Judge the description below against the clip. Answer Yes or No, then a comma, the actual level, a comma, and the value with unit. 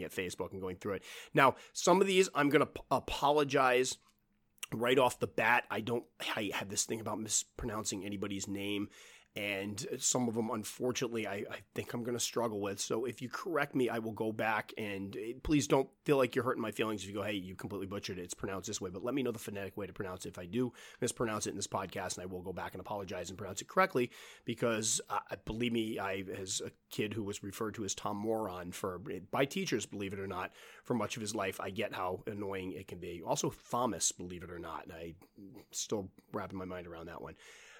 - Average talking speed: No, fast, 240 wpm